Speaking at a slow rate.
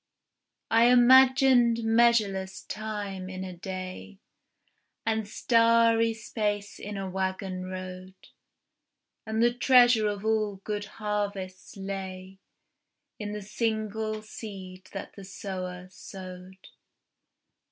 Yes: slow, 100 wpm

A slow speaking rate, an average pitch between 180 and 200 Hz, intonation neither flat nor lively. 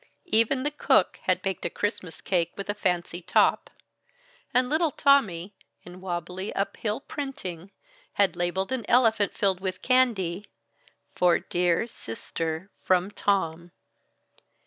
Yes: slow, 125 wpm; high, 190 Hz; average, 4.7 semitones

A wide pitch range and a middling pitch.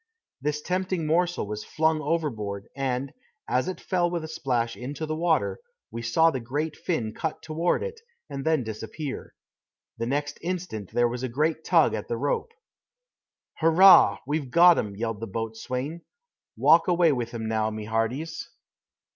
Yes: wide, 5.9 semitones; medium, 145 Hz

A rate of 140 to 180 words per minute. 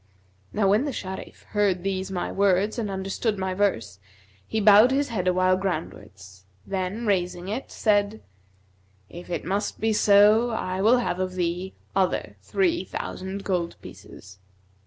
Yes: average, 150 wpm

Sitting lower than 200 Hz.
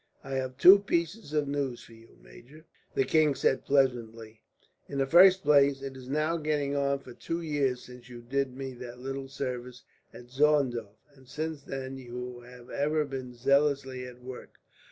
Yes: low, 135 Hz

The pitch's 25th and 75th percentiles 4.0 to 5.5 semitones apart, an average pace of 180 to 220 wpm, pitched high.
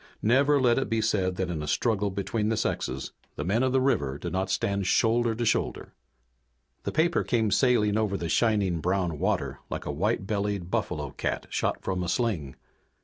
No: average, 4.3 semitones; average, 195 wpm; low, 100 Hz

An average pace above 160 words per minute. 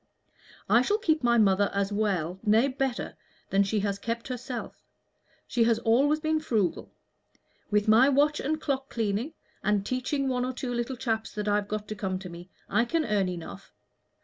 Yes: average, 180 wpm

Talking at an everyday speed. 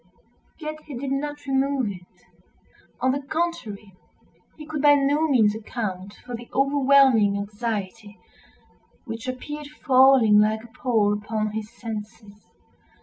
No: slow, 130 wpm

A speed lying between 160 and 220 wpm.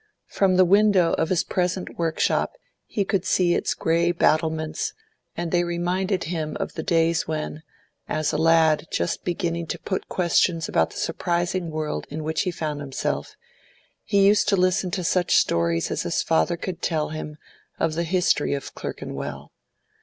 Yes: average, 170 wpm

